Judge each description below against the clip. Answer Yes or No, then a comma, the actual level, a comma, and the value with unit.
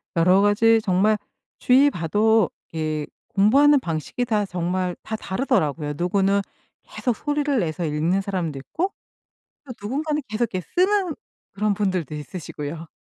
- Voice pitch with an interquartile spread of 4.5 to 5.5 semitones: No, wide, 6.3 semitones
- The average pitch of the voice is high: Yes, high, 200 Hz